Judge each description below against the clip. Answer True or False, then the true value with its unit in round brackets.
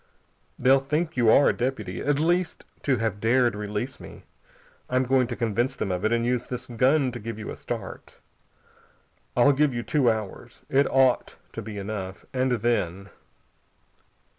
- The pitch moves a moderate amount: True (3.3 semitones)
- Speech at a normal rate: True (170 wpm)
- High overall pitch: False (120 Hz)